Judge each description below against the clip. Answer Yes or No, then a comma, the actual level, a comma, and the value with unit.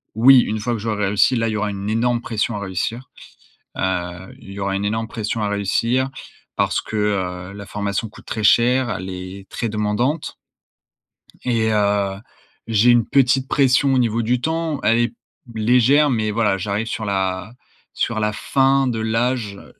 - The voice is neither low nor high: No, low, 110 Hz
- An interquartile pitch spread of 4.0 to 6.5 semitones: No, average, 3.2 semitones